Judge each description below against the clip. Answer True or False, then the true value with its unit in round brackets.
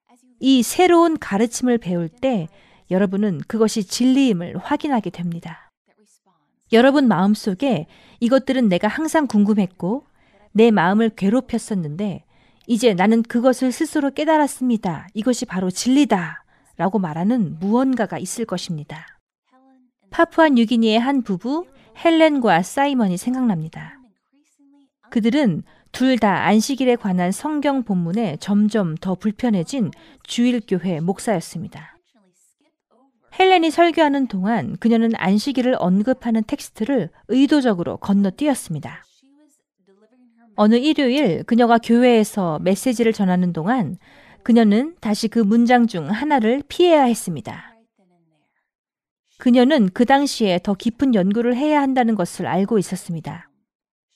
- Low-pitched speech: False (230 Hz)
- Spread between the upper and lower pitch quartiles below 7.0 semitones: True (5.2 semitones)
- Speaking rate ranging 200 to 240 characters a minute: False (285 characters per minute)